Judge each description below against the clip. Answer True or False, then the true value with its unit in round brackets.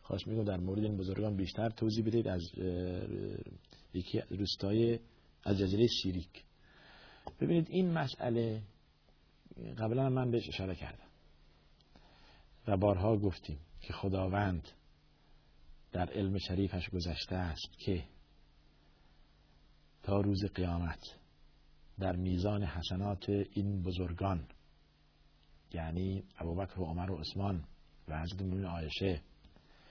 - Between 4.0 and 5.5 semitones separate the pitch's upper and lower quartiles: True (4.5 semitones)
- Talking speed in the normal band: False (100 wpm)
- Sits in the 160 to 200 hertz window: False (95 Hz)